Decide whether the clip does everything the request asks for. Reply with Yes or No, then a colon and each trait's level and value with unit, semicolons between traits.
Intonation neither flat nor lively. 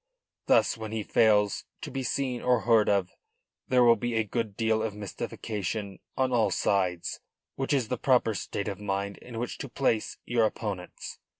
Yes: average, 3.0 semitones